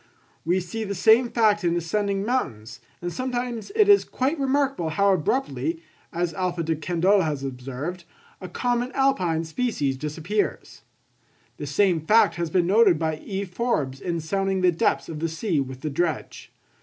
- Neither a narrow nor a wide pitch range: No, wide, 5.9 semitones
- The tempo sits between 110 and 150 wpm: No, average, 165 wpm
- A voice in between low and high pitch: Yes, medium, 180 Hz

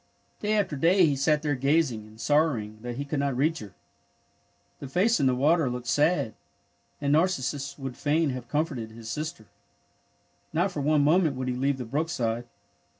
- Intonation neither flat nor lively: Yes, average, 4.3 semitones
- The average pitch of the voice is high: No, medium, 140 Hz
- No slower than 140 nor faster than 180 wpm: No, average, 190 wpm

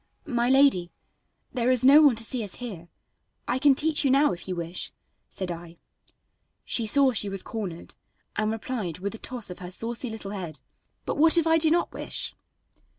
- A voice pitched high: Yes, high, 230 Hz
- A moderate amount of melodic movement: No, wide, 6.4 semitones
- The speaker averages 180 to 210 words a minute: Yes, average, 195 wpm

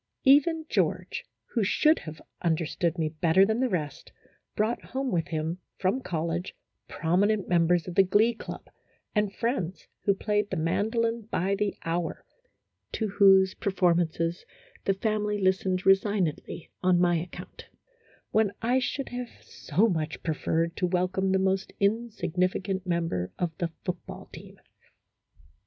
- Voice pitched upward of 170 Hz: Yes, high, 190 Hz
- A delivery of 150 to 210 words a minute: No, average, 140 wpm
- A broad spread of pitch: No, average, 3.6 semitones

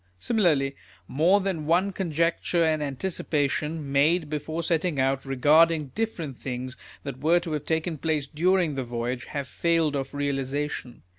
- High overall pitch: No, medium, 150 Hz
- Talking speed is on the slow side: No, average, 145 wpm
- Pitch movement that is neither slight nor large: Yes, average, 3.5 semitones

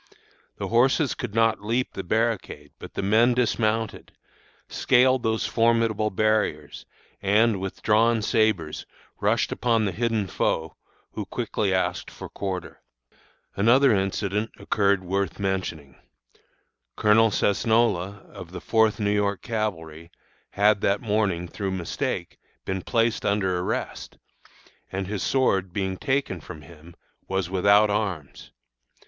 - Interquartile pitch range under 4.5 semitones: Yes, average, 3.1 semitones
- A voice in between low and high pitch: No, low, 105 Hz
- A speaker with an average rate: No, slow, 125 wpm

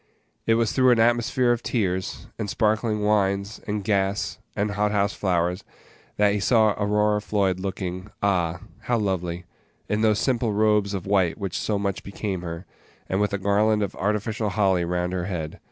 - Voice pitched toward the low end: Yes, low, 100 Hz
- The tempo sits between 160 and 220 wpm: Yes, average, 175 wpm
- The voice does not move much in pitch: Yes, narrow, 2.2 semitones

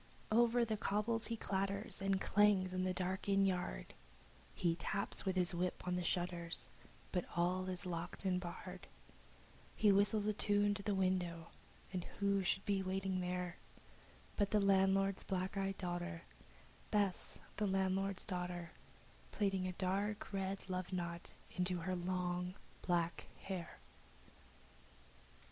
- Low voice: No, medium, 185 Hz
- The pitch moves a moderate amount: No, narrow, 1.8 semitones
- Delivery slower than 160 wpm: Yes, average, 140 wpm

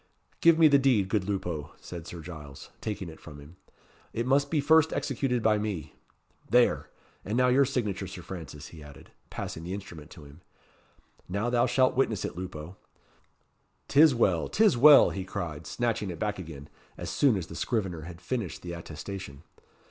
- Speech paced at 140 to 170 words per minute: No, average, 180 wpm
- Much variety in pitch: Yes, wide, 6.7 semitones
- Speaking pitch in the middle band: No, very low, 95 Hz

